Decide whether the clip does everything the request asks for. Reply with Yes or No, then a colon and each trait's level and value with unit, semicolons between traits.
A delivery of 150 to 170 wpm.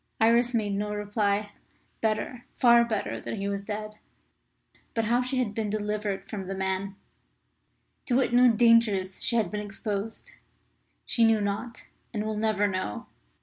Yes: average, 155 wpm